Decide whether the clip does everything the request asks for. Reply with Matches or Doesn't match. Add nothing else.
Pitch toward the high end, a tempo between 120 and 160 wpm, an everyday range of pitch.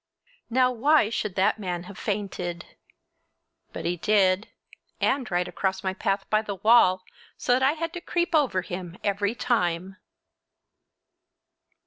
Matches